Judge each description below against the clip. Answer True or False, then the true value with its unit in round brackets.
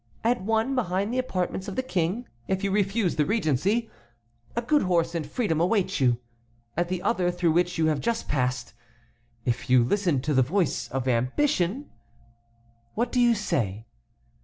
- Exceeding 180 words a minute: False (165 wpm)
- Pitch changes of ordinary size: False (8.7 semitones)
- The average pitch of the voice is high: False (180 Hz)